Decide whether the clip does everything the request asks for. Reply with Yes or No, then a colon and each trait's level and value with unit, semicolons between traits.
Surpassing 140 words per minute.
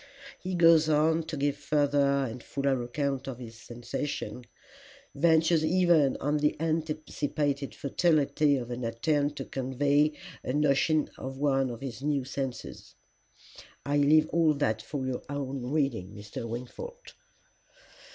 No: slow, 135 wpm